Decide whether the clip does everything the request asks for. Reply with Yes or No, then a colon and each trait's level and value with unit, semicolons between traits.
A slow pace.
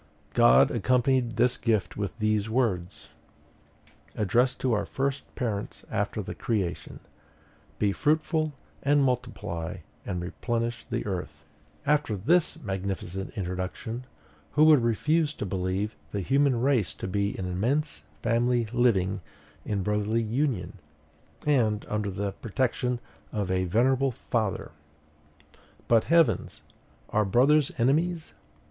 Yes: slow, 120 wpm